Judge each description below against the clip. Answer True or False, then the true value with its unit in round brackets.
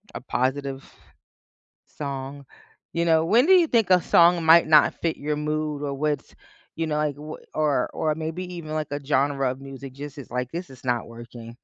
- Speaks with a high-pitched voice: False (150 Hz)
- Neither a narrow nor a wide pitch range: True (3.0 semitones)